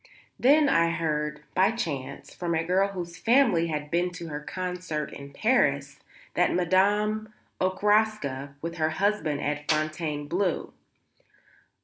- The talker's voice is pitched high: No, medium, 170 Hz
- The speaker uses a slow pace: Yes, slow, 130 wpm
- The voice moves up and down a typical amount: Yes, average, 4.8 semitones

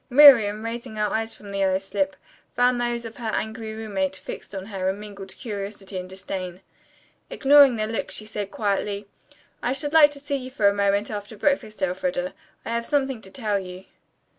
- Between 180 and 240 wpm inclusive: Yes, average, 190 wpm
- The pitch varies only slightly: No, average, 3.6 semitones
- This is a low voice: No, high, 210 Hz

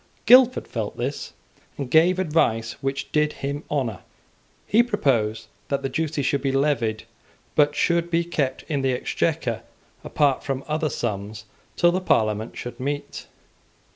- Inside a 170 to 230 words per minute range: No, average, 145 wpm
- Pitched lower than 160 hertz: Yes, medium, 140 Hz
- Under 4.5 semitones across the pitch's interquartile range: No, average, 4.8 semitones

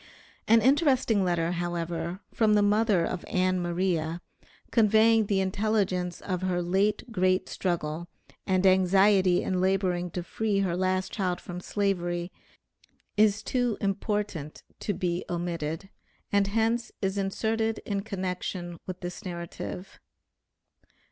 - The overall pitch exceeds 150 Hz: Yes, medium, 185 Hz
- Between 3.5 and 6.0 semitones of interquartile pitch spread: No, average, 2.8 semitones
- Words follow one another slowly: Yes, slow, 125 wpm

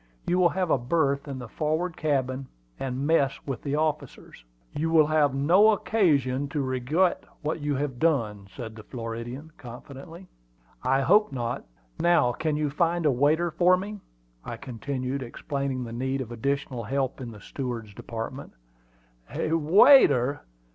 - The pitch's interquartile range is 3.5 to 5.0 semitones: Yes, average, 4.0 semitones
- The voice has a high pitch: No, medium, 140 Hz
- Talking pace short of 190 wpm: Yes, average, 155 wpm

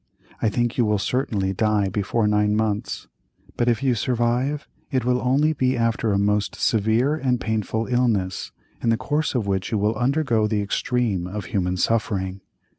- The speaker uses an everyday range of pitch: Yes, average, 3.2 semitones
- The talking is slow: No, average, 175 wpm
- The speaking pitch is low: Yes, low, 110 Hz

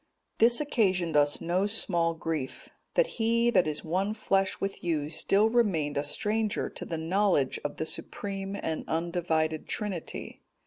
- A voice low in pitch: No, medium, 180 Hz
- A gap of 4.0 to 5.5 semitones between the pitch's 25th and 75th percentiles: Yes, average, 4.6 semitones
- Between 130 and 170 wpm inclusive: Yes, average, 150 wpm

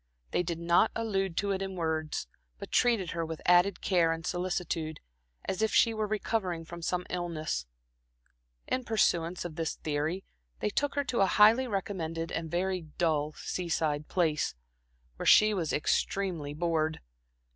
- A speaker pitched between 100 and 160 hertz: No, medium, 175 Hz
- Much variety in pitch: No, average, 3.4 semitones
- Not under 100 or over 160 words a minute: Yes, average, 155 wpm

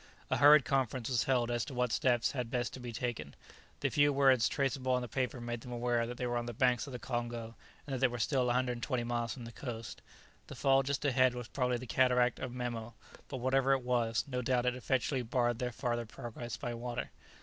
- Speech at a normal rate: No, fast, 225 wpm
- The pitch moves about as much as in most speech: No, narrow, 1.6 semitones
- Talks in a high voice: No, low, 125 Hz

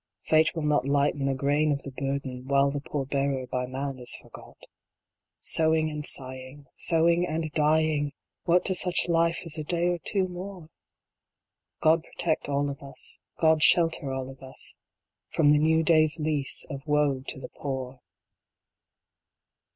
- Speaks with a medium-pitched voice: Yes, medium, 150 Hz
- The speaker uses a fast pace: No, average, 165 wpm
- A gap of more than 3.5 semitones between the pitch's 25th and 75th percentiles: No, average, 2.7 semitones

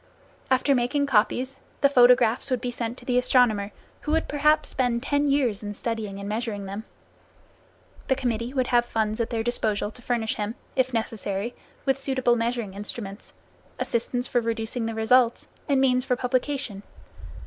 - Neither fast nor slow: Yes, average, 165 wpm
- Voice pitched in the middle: No, high, 240 Hz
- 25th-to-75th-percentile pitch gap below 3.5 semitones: Yes, average, 2.7 semitones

